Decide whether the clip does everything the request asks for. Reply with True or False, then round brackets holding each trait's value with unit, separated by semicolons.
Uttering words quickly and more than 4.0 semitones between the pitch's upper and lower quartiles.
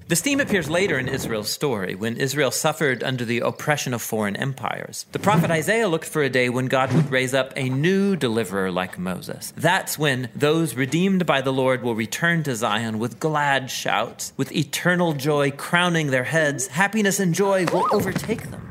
False (190 wpm; 4.8 semitones)